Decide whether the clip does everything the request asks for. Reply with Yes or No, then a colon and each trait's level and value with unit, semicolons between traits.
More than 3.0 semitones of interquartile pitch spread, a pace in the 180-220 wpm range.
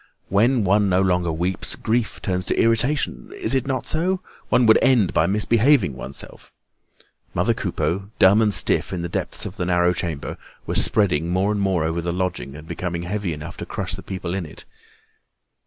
Yes: average, 4.2 semitones; average, 190 wpm